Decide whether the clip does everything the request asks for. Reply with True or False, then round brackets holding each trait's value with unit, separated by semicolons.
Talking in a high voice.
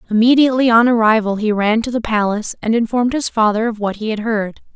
True (225 Hz)